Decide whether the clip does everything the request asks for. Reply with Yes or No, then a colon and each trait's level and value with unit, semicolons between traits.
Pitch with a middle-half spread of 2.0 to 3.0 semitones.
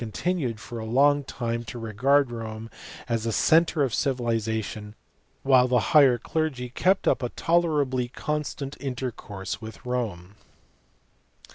No: average, 3.9 semitones